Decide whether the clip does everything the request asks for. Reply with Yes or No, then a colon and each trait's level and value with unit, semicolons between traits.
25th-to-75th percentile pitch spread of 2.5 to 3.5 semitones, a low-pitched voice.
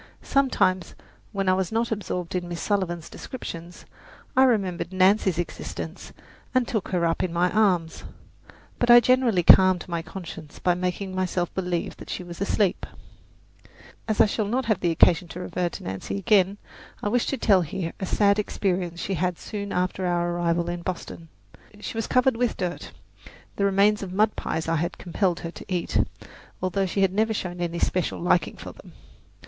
No: average, 2.9 semitones; medium, 185 Hz